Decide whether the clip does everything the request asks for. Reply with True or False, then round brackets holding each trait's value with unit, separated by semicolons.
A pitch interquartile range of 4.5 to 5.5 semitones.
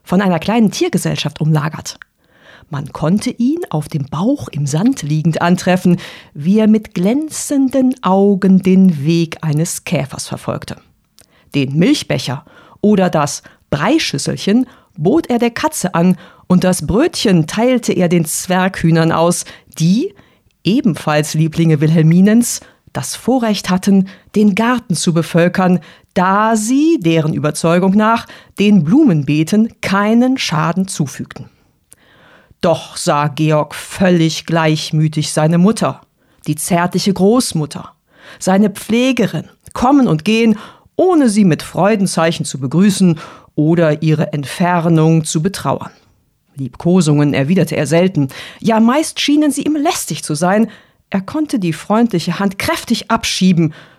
True (5.2 semitones)